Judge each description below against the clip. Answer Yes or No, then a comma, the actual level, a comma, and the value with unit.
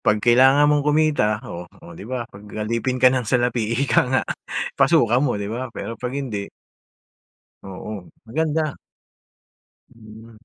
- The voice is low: Yes, low, 120 Hz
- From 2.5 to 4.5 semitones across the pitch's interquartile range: Yes, average, 3.9 semitones